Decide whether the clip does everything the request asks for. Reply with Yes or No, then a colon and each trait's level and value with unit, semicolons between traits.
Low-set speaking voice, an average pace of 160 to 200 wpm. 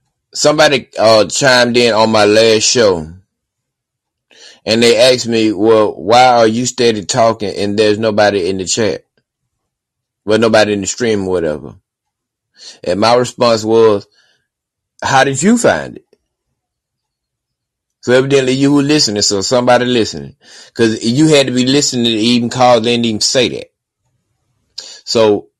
No: low, 115 Hz; average, 150 wpm